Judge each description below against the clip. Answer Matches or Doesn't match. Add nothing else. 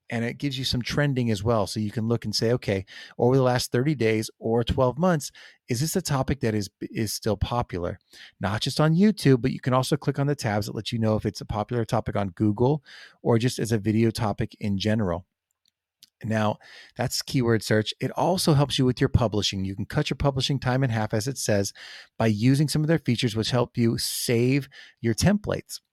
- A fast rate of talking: Matches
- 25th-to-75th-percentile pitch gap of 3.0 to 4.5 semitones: Matches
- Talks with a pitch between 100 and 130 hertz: Matches